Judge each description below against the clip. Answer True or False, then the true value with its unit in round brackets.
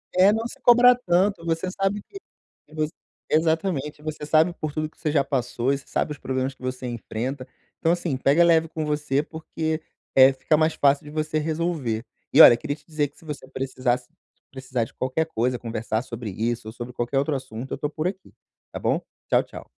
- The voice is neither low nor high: True (150 Hz)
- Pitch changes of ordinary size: True (4.0 semitones)